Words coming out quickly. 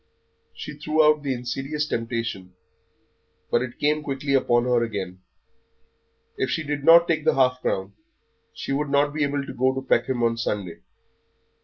No: average, 160 wpm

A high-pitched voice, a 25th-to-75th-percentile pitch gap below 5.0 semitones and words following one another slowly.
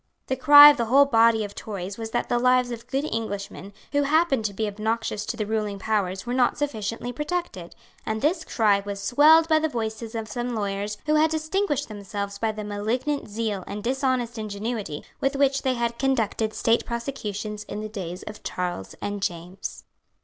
No: high, 225 Hz; average, 4.4 semitones; average, 190 wpm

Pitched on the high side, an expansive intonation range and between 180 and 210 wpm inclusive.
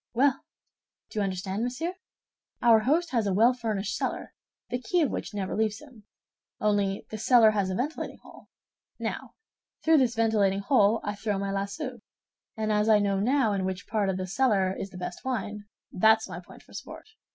No: high, 215 Hz; average, 3.8 semitones; average, 190 wpm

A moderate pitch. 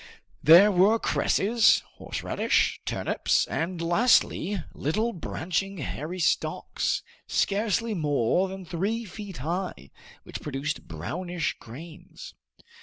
Yes: medium, 180 Hz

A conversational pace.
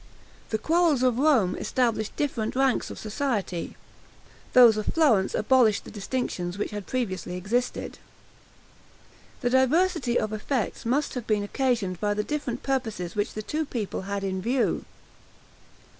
Yes: average, 145 wpm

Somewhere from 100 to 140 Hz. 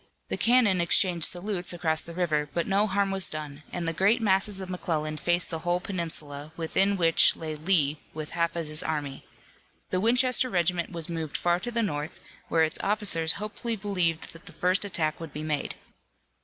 No: medium, 175 Hz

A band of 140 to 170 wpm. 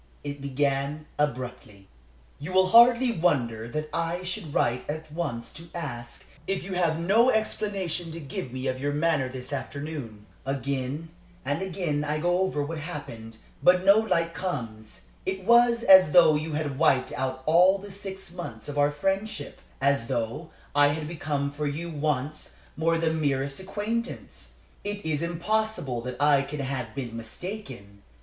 Yes: average, 165 wpm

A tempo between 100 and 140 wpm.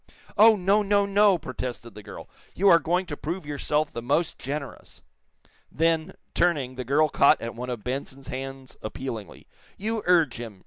No: average, 170 wpm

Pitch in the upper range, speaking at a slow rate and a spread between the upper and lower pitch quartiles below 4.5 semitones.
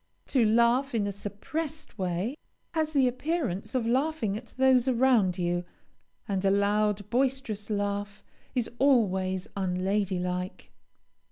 No: high, 215 Hz; slow, 125 wpm; average, 5.0 semitones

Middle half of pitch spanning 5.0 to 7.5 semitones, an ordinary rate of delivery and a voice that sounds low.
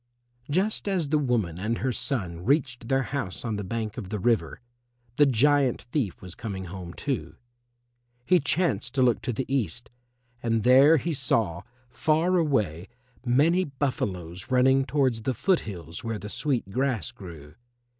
Yes: wide, 5.6 semitones; average, 160 wpm; low, 125 Hz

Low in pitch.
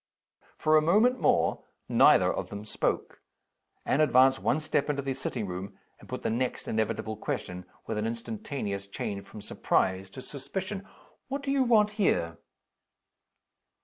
Yes: low, 130 Hz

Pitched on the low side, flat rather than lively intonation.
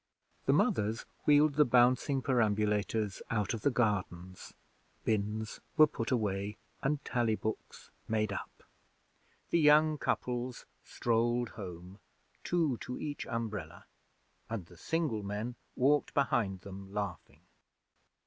No: low, 115 Hz; average, 4.2 semitones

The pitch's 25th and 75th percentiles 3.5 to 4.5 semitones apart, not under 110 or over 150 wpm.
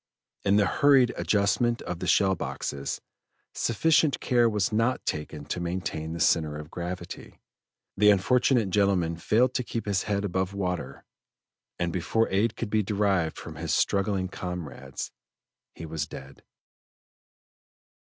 Yes: average, 4.2 semitones; average, 140 wpm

